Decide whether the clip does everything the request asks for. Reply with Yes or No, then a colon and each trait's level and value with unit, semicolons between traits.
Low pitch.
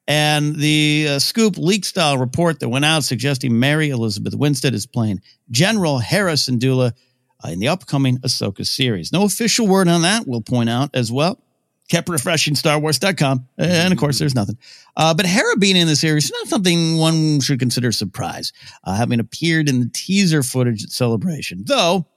No: medium, 150 Hz